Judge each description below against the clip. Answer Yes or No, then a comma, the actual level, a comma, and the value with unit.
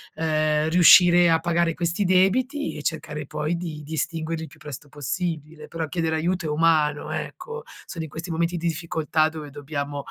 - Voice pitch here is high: No, medium, 160 Hz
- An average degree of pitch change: No, narrow, 2.1 semitones